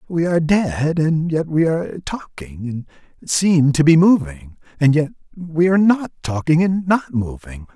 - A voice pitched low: No, medium, 155 Hz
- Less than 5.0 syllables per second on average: Yes, 4.3 syllables/s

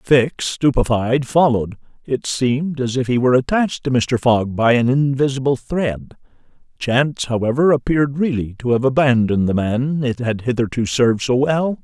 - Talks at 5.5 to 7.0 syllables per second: No, 5.1 syllables/s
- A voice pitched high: No, low, 130 Hz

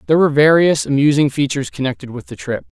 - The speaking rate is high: No, average, 195 wpm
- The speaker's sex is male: Yes, male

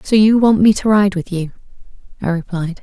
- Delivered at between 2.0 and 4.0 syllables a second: No, 5.4 syllables/s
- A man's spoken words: No, female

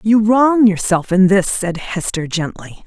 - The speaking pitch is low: No, high, 195 Hz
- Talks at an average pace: Yes, average, 165 wpm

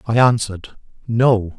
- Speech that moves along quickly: No, slow, 115 wpm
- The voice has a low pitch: Yes, low, 110 Hz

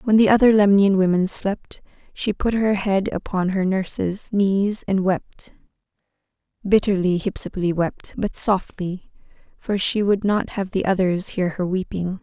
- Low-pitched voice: No, high, 195 Hz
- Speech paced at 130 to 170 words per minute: Yes, average, 150 wpm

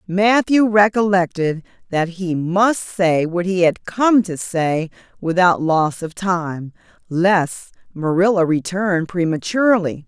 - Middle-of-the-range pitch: Yes, medium, 180 Hz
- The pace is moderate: No, slow, 120 wpm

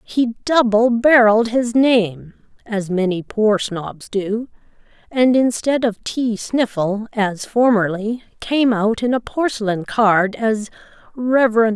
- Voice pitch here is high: Yes, high, 225 Hz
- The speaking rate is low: Yes, slow, 130 wpm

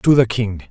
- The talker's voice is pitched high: No, low, 110 Hz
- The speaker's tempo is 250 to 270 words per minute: Yes, fast, 255 wpm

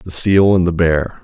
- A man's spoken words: Yes, male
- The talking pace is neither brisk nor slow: No, fast, 245 wpm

